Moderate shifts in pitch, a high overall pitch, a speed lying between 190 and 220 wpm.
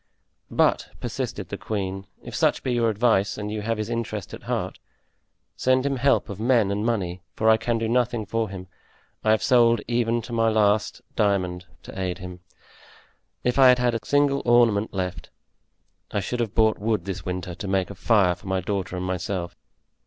No: average, 3.7 semitones; low, 110 Hz; average, 195 wpm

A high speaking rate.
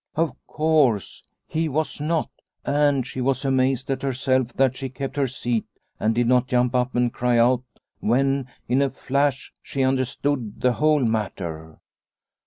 No: average, 160 wpm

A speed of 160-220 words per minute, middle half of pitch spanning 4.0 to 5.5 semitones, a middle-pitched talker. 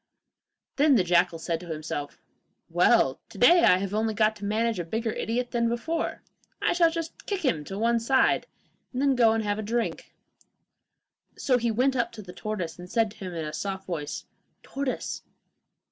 No: average, 190 wpm; average, 5.2 semitones; high, 220 Hz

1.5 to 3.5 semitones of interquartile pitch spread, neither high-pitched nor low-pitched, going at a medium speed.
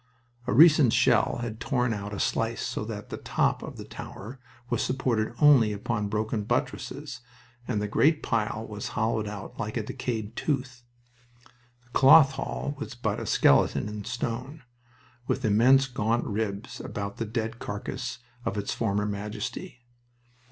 No: average, 3.2 semitones; low, 115 Hz; average, 155 wpm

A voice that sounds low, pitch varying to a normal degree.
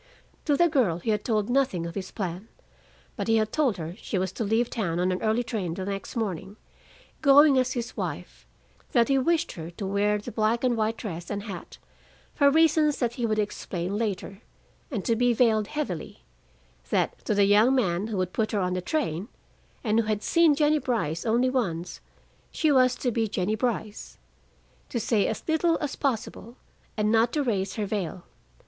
No: high, 220 Hz; average, 4.4 semitones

